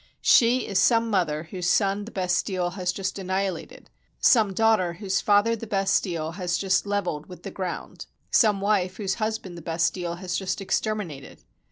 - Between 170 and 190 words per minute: Yes, average, 175 wpm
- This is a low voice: No, high, 190 Hz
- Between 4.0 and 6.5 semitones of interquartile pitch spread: No, narrow, 2.6 semitones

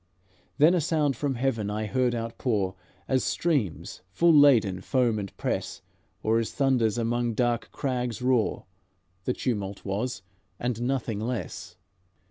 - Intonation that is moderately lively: Yes, average, 3.3 semitones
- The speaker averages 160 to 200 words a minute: No, slow, 135 wpm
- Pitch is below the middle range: Yes, low, 120 Hz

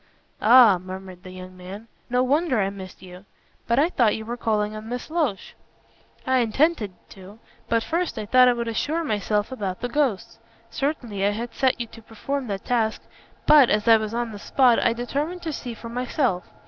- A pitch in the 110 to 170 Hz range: No, high, 230 Hz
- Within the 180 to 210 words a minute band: Yes, average, 200 wpm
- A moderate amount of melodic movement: Yes, average, 3.9 semitones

